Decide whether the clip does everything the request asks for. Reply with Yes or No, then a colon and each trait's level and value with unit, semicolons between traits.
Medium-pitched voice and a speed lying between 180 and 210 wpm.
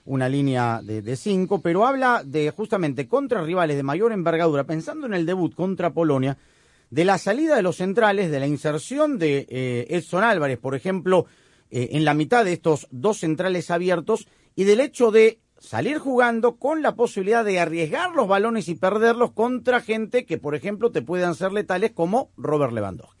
Yes: medium, 180 Hz; average, 185 wpm